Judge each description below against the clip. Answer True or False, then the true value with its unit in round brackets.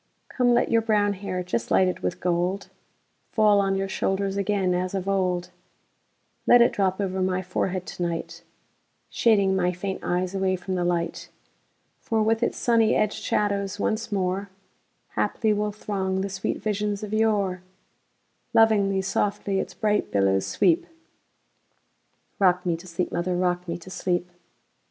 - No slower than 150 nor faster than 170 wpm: False (135 wpm)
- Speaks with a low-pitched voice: False (195 Hz)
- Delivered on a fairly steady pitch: True (2.3 semitones)